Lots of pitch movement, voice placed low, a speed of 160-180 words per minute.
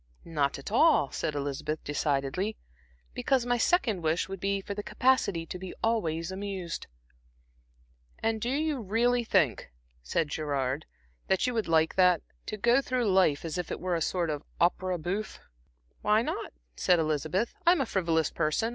No: wide, 6.0 semitones; medium, 185 Hz; average, 165 wpm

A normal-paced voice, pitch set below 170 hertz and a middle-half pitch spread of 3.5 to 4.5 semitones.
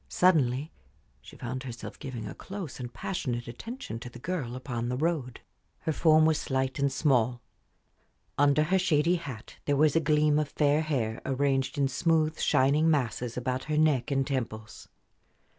Yes: average, 165 wpm; medium, 140 Hz; average, 3.8 semitones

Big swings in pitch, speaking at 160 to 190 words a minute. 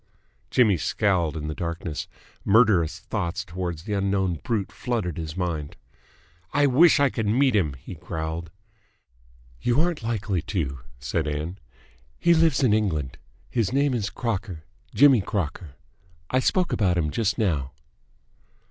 No: wide, 6.0 semitones; average, 140 wpm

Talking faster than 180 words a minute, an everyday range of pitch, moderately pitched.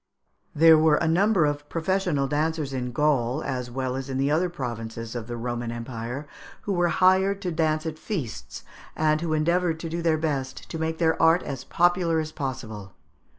Yes: average, 190 wpm; average, 4.4 semitones; medium, 155 Hz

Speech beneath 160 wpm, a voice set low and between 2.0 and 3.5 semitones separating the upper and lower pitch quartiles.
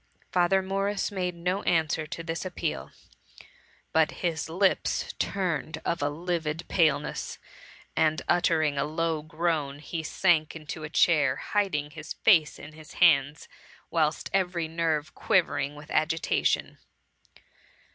No: slow, 135 wpm; medium, 160 Hz; narrow, 2.5 semitones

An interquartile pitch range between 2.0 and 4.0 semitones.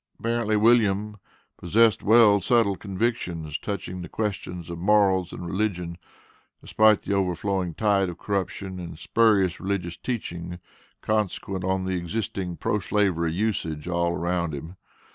Yes: average, 3.3 semitones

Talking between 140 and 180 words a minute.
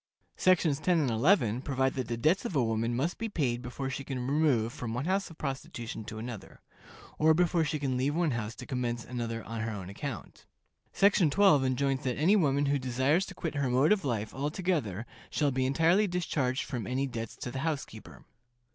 No: fast, 205 wpm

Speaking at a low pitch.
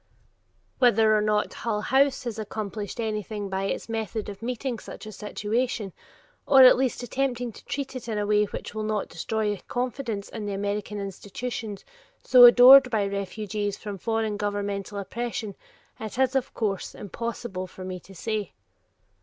No: high, 215 Hz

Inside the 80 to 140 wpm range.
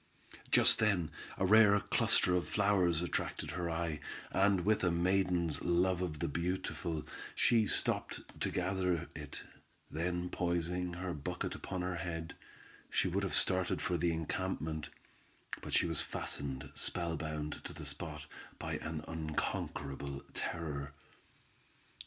Yes: slow, 135 wpm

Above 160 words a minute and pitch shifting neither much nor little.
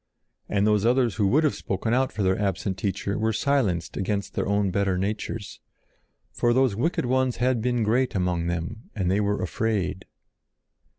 Yes: average, 175 wpm; average, 3.9 semitones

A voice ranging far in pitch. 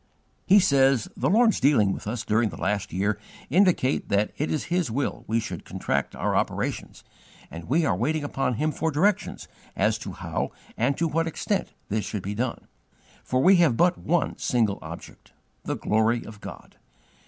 Yes: wide, 7.3 semitones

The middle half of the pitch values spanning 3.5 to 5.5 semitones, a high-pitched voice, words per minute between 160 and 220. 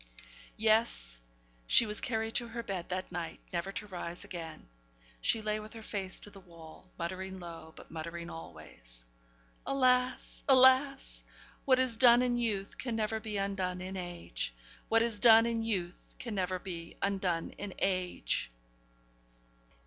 No: average, 4.6 semitones; high, 195 Hz; average, 150 wpm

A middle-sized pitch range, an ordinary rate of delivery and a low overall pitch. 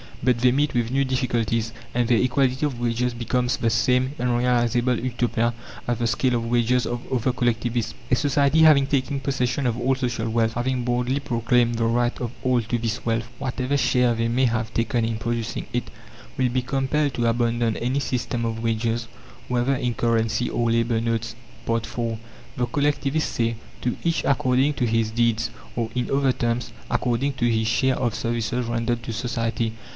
No: narrow, 1.7 semitones; average, 180 wpm; low, 120 Hz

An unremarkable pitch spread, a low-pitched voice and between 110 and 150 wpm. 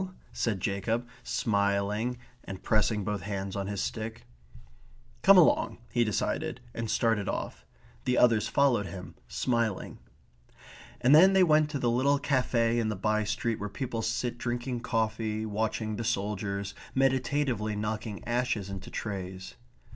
Yes: average, 3.1 semitones; low, 110 Hz; average, 140 wpm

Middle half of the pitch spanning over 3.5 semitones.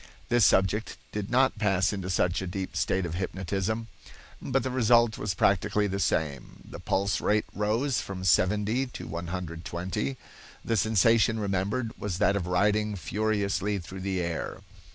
No: average, 3.0 semitones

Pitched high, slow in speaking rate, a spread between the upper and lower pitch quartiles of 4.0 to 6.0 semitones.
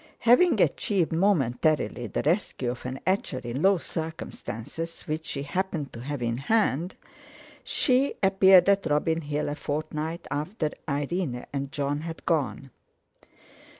No: medium, 155 Hz; slow, 125 wpm; average, 4.8 semitones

